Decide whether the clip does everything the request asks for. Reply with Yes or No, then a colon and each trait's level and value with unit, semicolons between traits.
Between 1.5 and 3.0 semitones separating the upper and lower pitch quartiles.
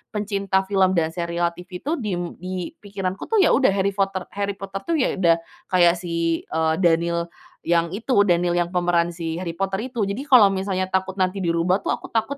Yes: narrow, 2.5 semitones